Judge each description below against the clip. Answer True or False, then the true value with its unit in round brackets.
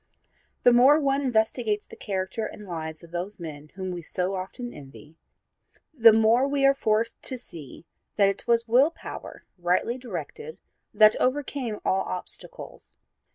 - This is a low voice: False (215 Hz)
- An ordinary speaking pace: True (155 wpm)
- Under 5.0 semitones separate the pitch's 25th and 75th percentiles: False (5.6 semitones)